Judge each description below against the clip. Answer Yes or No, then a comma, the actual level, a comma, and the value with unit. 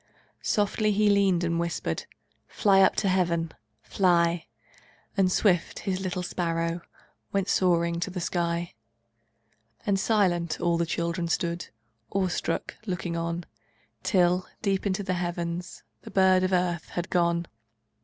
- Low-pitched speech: No, medium, 175 Hz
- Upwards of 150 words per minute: No, slow, 135 wpm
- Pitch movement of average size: No, narrow, 1.9 semitones